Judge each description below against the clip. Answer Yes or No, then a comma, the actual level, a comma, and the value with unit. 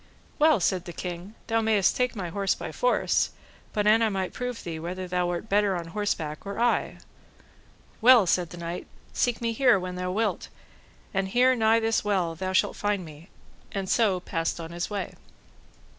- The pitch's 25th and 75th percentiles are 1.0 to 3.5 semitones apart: No, average, 4.1 semitones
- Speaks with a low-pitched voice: No, high, 195 Hz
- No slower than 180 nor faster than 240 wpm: Yes, average, 185 wpm